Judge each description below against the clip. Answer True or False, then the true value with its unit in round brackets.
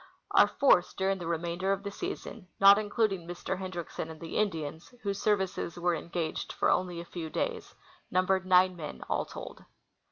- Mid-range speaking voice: True (180 Hz)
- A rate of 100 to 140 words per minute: False (170 wpm)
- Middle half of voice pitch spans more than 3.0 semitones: False (2.4 semitones)